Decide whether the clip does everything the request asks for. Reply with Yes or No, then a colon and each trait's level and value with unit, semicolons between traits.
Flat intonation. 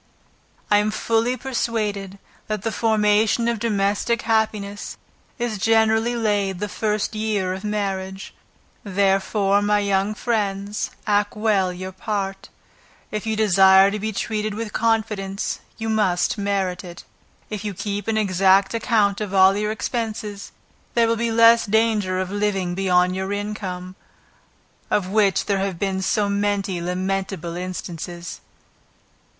Yes: narrow, 2.2 semitones